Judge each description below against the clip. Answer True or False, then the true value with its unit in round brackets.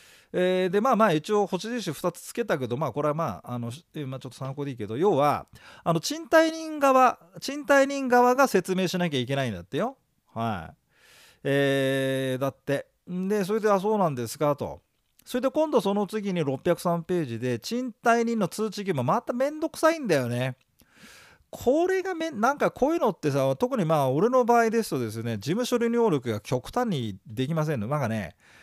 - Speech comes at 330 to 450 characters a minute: True (355 characters per minute)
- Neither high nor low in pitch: True (180 Hz)